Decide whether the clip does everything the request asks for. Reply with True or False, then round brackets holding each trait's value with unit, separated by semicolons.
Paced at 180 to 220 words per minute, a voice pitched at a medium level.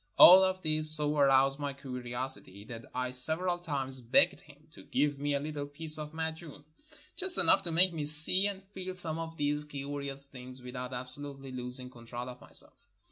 True (190 wpm; 145 Hz)